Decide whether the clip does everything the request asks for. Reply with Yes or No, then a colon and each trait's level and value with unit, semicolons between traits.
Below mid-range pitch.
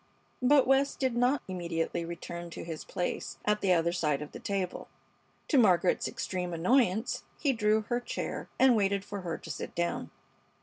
No: high, 195 Hz